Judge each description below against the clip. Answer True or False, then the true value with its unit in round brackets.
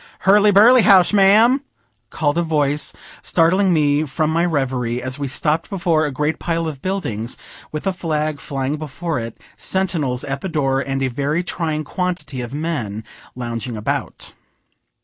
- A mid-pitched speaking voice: True (150 Hz)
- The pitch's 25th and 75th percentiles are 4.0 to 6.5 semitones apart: True (4.5 semitones)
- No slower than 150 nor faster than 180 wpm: True (160 wpm)